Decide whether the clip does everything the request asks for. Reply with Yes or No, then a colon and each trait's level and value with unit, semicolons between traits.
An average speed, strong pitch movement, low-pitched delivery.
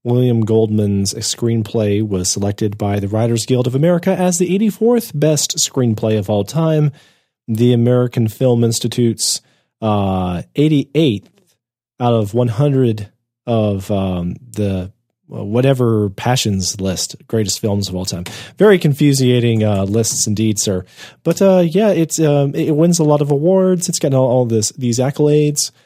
Yes: average, 155 wpm; wide, 5.7 semitones; low, 120 Hz